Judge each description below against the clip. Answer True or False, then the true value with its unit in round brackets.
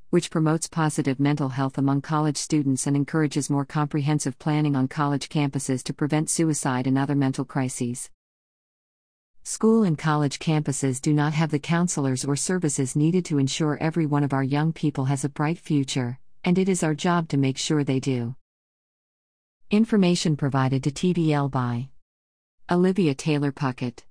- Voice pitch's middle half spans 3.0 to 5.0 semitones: False (2.6 semitones)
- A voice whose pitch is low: False (145 Hz)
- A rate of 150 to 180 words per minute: True (160 wpm)